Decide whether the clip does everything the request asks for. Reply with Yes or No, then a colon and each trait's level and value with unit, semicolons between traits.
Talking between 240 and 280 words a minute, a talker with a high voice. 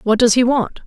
Yes: fast, 275 wpm; high, 235 Hz